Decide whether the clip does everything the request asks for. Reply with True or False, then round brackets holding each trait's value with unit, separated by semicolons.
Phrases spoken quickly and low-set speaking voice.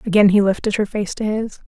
False (245 wpm; 205 Hz)